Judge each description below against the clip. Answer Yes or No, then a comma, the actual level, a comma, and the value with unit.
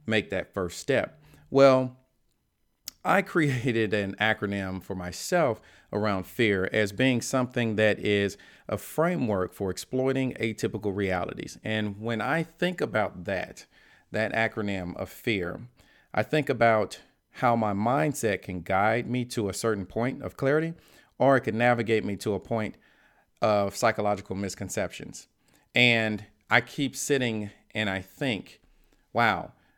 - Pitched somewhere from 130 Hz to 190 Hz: No, low, 110 Hz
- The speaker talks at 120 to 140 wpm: Yes, slow, 135 wpm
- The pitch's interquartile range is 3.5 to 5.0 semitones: Yes, average, 3.8 semitones